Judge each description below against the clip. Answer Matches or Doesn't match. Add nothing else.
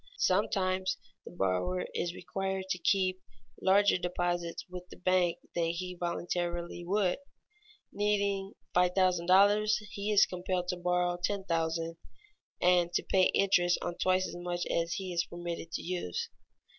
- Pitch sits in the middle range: Matches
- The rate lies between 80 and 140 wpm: Matches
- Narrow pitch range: Matches